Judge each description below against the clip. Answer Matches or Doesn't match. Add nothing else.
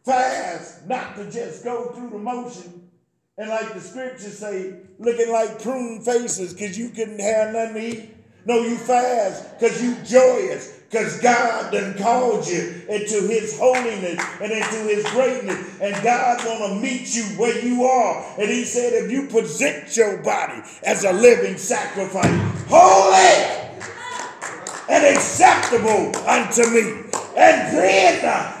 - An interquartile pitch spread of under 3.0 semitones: Matches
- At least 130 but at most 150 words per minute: Matches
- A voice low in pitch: Doesn't match